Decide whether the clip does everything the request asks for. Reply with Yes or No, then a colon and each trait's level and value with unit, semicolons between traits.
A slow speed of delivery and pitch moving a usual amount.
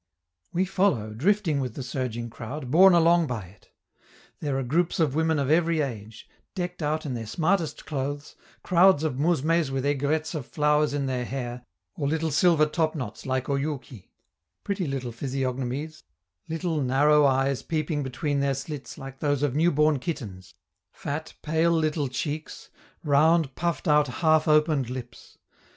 No: average, 155 wpm; average, 3.4 semitones